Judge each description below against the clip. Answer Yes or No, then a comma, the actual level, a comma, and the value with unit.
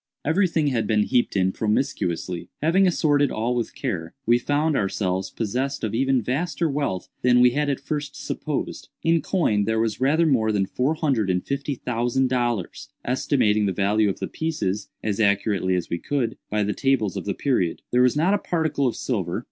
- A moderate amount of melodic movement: No, wide, 5.7 semitones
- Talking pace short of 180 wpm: No, average, 190 wpm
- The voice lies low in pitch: Yes, low, 120 Hz